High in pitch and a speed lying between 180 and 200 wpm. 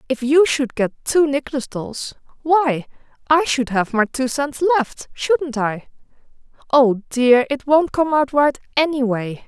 No: very high, 270 Hz; average, 160 wpm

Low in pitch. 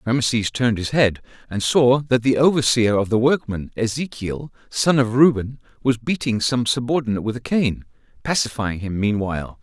Yes: low, 120 Hz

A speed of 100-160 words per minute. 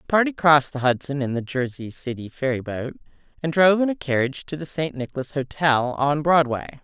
No: average, 195 wpm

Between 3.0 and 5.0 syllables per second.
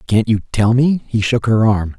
Yes: 4.6 syllables/s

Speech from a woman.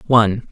No: male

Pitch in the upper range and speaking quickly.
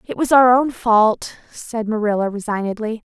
No: high, 225 Hz; average, 155 wpm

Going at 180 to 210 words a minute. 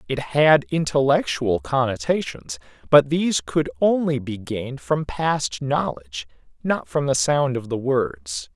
No: average, 140 wpm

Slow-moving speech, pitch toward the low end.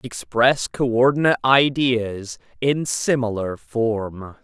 Yes: slow, 95 wpm; low, 120 Hz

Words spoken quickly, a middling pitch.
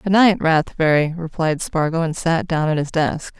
No: average, 195 wpm; medium, 165 Hz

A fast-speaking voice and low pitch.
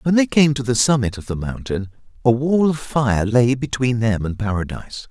Yes: fast, 210 wpm; low, 120 Hz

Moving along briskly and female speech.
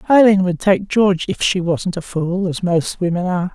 Yes: fast, 220 wpm; female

